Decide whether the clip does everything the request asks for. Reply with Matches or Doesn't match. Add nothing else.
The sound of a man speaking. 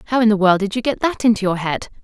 Doesn't match